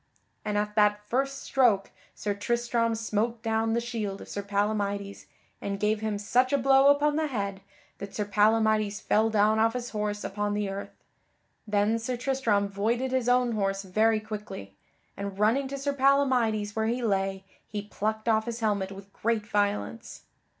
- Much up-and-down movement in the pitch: No, narrow, 2.6 semitones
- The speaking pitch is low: No, high, 215 Hz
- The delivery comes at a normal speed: Yes, average, 170 wpm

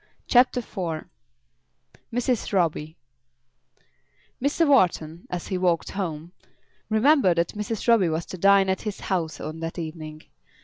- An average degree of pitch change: Yes, average, 4.9 semitones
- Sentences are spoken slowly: Yes, slow, 130 wpm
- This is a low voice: No, medium, 185 Hz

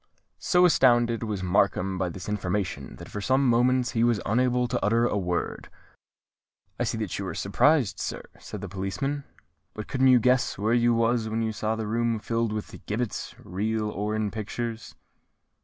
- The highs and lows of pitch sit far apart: No, average, 2.9 semitones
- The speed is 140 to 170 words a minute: No, average, 180 wpm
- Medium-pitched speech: No, low, 110 Hz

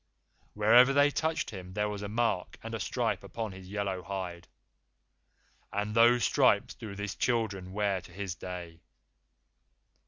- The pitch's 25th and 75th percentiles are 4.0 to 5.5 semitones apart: No, average, 3.4 semitones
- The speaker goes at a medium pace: Yes, average, 150 wpm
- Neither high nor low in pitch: No, low, 100 Hz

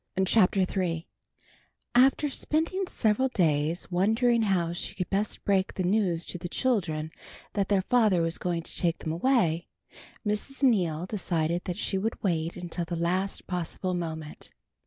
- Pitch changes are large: No, average, 4.0 semitones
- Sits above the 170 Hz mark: Yes, medium, 185 Hz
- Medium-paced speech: Yes, average, 155 wpm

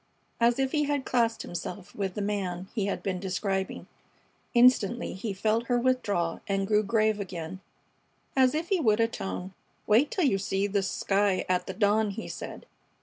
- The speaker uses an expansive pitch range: No, average, 3.6 semitones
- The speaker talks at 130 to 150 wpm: No, average, 175 wpm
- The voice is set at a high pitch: Yes, high, 205 Hz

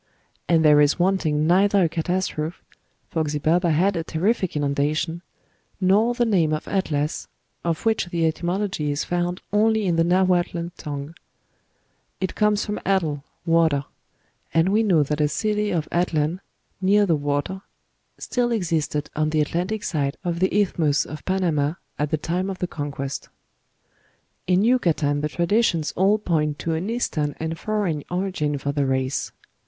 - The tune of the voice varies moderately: Yes, average, 4.0 semitones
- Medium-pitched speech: Yes, medium, 170 Hz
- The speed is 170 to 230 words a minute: No, average, 155 wpm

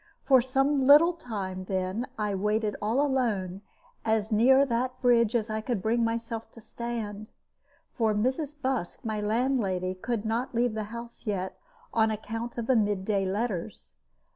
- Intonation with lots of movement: No, average, 2.9 semitones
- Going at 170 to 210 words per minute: No, average, 160 wpm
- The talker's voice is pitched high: Yes, high, 225 Hz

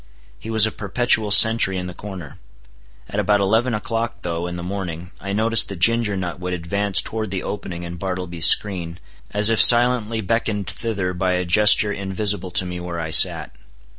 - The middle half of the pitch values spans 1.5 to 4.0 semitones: Yes, average, 3.5 semitones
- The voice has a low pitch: Yes, low, 100 Hz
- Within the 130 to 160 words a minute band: No, average, 185 wpm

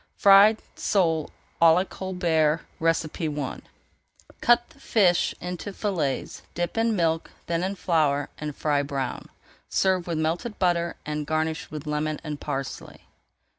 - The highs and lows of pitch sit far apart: No, average, 3.8 semitones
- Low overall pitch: No, medium, 165 Hz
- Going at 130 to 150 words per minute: Yes, slow, 135 wpm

